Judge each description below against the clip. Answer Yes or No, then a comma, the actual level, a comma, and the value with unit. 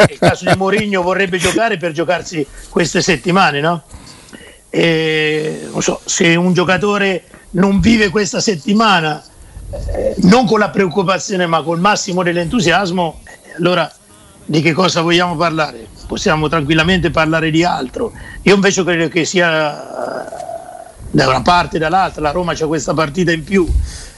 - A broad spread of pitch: No, average, 3.3 semitones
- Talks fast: No, average, 140 wpm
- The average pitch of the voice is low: No, medium, 175 Hz